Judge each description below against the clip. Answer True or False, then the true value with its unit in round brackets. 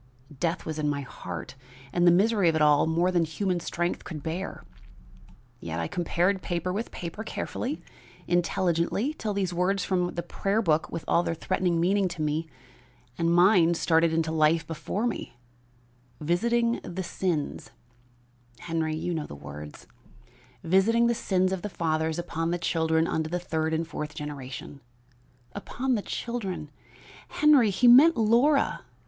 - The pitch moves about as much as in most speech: True (3.5 semitones)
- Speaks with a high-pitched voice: False (170 Hz)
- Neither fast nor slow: True (160 wpm)